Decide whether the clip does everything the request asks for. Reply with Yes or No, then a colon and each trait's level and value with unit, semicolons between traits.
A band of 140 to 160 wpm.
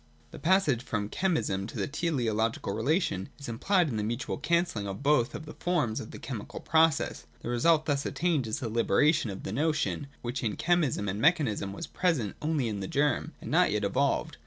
No: average, 200 wpm